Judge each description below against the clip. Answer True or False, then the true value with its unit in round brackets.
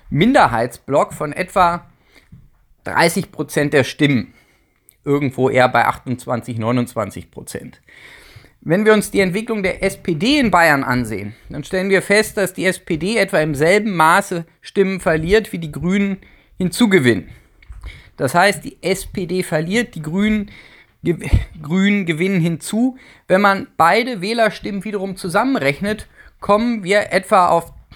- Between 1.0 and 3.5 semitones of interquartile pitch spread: False (5.2 semitones)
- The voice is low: False (185 Hz)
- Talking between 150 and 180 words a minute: False (125 wpm)